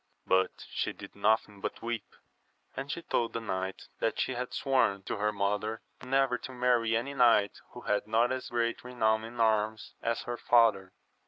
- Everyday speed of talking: Yes, average, 180 wpm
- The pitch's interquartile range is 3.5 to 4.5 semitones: No, average, 2.7 semitones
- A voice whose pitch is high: No, low, 115 Hz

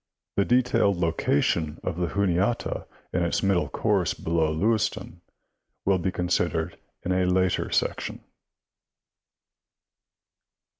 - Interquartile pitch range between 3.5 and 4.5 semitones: No, average, 2.8 semitones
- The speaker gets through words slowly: Yes, slow, 110 wpm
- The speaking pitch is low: Yes, very low, 90 Hz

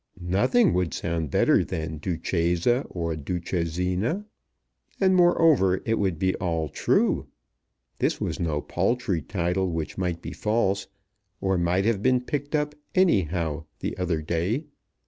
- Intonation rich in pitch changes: Yes, wide, 5.7 semitones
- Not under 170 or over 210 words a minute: No, average, 140 wpm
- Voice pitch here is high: No, very low, 90 Hz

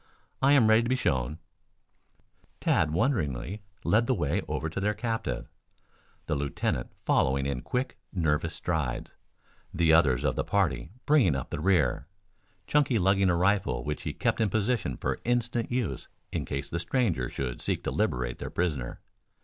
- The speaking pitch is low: Yes, very low, 85 Hz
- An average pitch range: No, wide, 8.2 semitones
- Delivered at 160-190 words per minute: Yes, average, 165 wpm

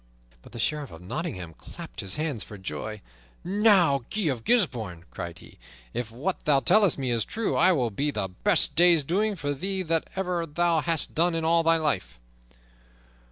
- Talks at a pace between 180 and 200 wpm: Yes, average, 185 wpm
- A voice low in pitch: No, medium, 155 Hz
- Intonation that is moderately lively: No, wide, 7.5 semitones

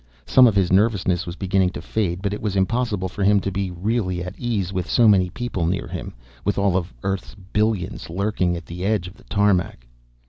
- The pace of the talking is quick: Yes, fast, 215 wpm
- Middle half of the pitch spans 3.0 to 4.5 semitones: No, narrow, 2.6 semitones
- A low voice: Yes, very low, 95 Hz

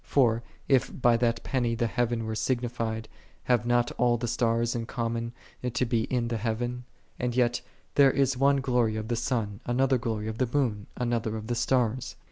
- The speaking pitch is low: Yes, low, 120 Hz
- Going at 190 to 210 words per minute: Yes, average, 195 wpm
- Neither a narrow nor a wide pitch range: No, narrow, 1.5 semitones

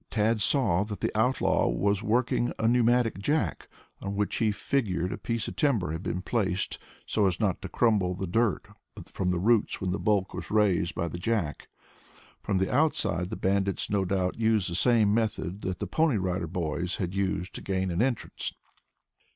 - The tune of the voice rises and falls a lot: No, average, 3.7 semitones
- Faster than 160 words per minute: Yes, average, 190 wpm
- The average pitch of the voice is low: Yes, low, 100 Hz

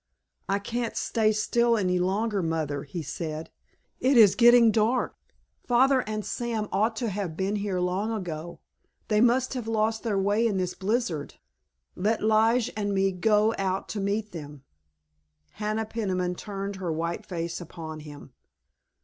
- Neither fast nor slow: Yes, average, 155 wpm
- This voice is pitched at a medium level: No, high, 205 Hz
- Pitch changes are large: No, average, 3.7 semitones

